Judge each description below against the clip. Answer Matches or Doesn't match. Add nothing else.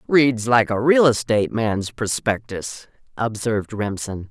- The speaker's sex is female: Matches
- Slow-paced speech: Matches